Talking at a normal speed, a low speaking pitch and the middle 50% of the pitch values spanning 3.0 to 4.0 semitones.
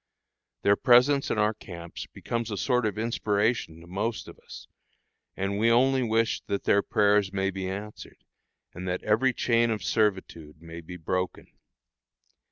Yes: average, 160 wpm; low, 105 Hz; average, 3.7 semitones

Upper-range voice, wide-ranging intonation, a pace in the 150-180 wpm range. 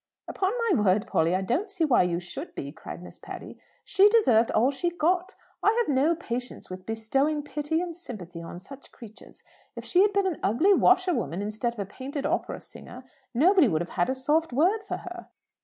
No: very high, 275 Hz; wide, 9.0 semitones; fast, 205 wpm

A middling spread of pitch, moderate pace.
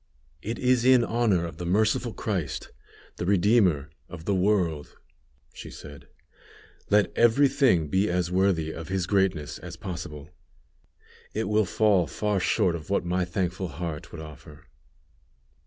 Yes: average, 4.2 semitones; average, 145 wpm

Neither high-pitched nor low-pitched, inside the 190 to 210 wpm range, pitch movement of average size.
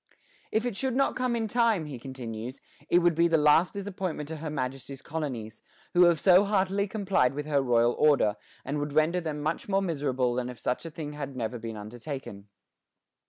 No: medium, 150 Hz; average, 200 wpm; wide, 6.1 semitones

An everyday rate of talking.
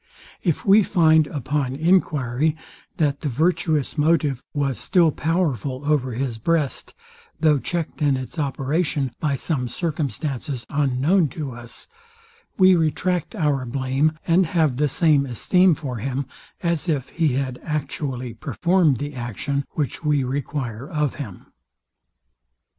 No: slow, 130 wpm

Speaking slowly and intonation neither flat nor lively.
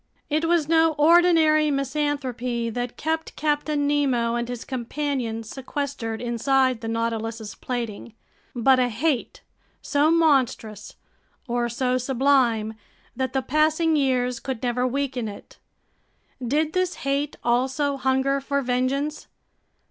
Yes: slow, 120 wpm; average, 3.6 semitones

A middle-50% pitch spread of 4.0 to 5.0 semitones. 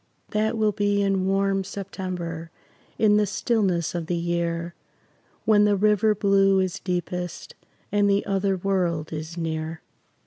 No: average, 2.9 semitones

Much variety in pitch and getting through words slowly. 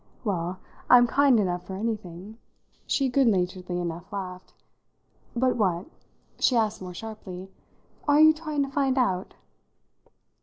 Yes: wide, 5.9 semitones; slow, 125 wpm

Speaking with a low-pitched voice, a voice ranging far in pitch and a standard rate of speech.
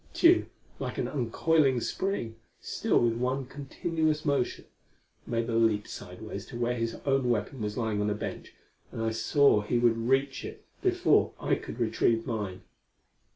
No: low, 120 Hz; average, 3.4 semitones; average, 160 wpm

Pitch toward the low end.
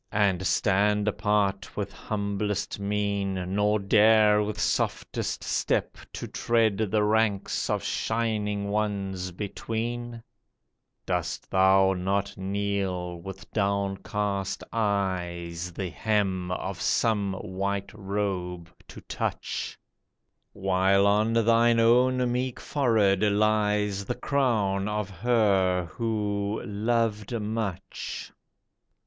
Yes: low, 100 Hz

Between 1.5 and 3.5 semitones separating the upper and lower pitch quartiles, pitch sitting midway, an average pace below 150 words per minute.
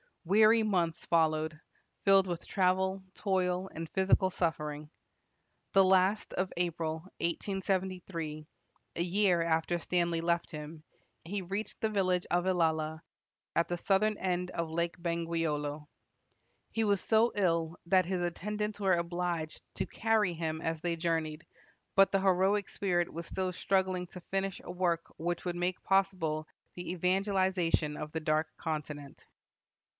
Yes: narrow, 2.6 semitones; medium, 175 Hz; average, 140 wpm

